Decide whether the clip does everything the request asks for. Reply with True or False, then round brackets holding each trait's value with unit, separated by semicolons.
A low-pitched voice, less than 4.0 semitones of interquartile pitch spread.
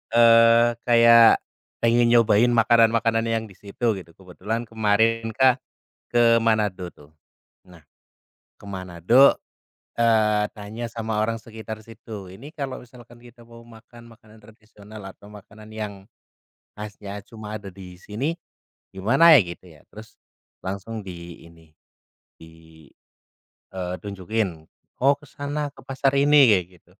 True (110 Hz; 2.9 semitones)